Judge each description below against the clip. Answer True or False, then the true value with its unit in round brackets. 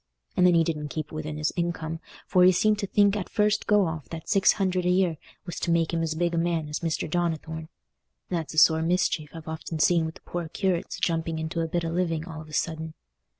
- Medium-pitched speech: True (165 Hz)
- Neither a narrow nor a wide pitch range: False (2.0 semitones)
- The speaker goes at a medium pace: False (245 wpm)